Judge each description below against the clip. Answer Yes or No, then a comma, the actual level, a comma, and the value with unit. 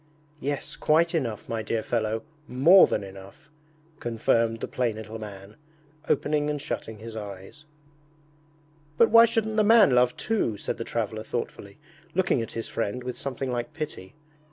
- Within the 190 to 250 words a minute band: No, average, 155 wpm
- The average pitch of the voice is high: No, low, 120 Hz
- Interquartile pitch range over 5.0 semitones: Yes, wide, 5.5 semitones